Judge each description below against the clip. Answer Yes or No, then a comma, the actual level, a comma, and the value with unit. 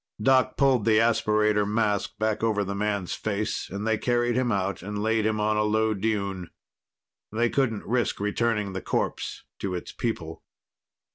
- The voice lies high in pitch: No, low, 105 Hz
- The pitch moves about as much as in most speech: No, narrow, 1.9 semitones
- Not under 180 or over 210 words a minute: No, average, 165 wpm